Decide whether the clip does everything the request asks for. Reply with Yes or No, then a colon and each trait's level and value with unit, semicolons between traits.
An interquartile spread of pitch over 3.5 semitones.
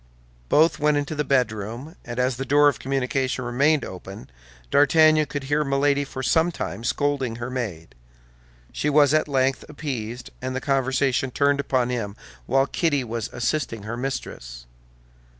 No: average, 3.2 semitones